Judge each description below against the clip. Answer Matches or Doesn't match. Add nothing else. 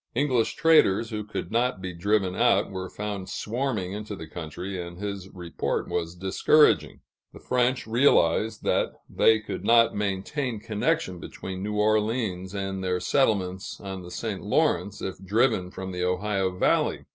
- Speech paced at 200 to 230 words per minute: Doesn't match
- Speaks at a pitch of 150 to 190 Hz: Doesn't match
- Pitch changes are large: Doesn't match